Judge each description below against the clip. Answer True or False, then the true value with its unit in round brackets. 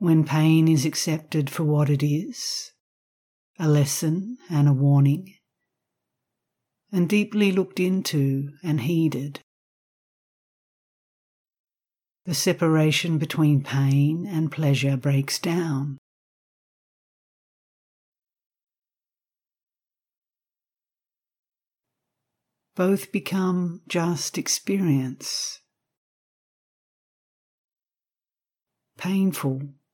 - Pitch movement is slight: False (4.1 semitones)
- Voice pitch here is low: False (155 Hz)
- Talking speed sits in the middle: False (65 wpm)